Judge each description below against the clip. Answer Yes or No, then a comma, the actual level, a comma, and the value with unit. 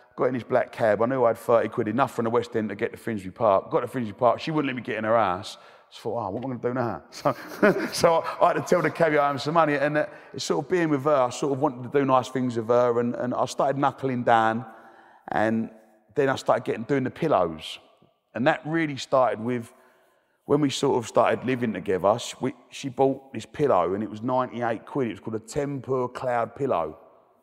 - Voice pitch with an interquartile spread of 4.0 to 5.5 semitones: No, average, 3.5 semitones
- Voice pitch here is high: No, low, 125 Hz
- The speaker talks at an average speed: No, fast, 255 wpm